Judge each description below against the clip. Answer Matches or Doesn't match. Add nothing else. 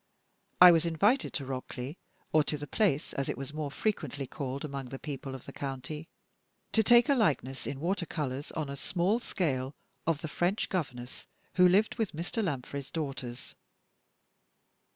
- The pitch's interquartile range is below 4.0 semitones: Doesn't match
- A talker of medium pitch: Matches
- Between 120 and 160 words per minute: Doesn't match